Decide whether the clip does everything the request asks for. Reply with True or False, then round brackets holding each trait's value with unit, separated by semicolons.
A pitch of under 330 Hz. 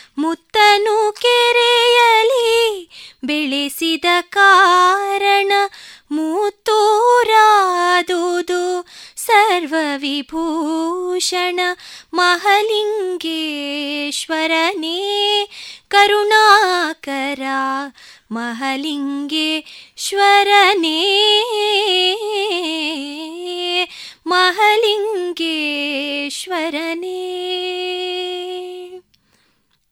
False (360 Hz)